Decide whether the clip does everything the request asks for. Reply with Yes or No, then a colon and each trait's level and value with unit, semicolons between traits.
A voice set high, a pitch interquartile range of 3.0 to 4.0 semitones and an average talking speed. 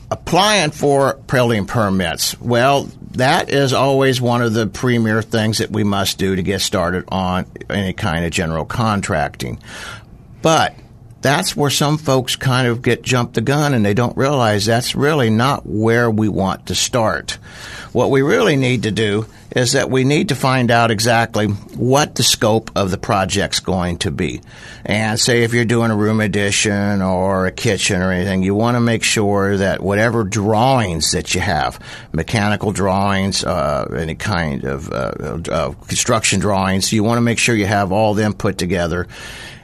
No: low, 110 Hz; average, 3.5 semitones; average, 175 wpm